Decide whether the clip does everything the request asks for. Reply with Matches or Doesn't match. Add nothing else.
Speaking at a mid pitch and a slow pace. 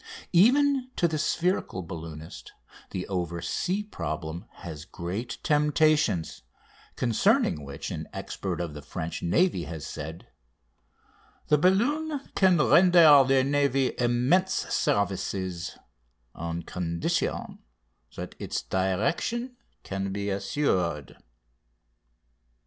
Doesn't match